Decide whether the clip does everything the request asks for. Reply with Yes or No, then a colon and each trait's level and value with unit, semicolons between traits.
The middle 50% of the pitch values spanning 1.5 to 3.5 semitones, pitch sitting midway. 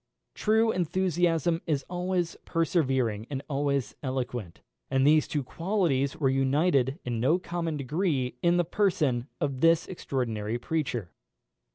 No: average, 4.8 semitones; medium, 145 Hz